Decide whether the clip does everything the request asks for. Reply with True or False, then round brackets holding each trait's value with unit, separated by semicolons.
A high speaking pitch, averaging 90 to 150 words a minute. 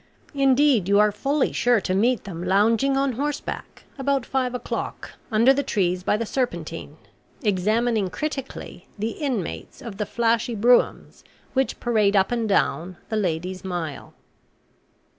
True (225 Hz; 140 wpm)